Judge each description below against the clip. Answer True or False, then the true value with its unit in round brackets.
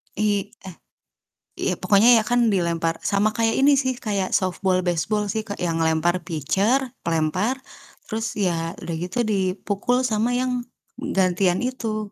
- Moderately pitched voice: False (200 Hz)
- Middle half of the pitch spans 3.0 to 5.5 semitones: True (3.8 semitones)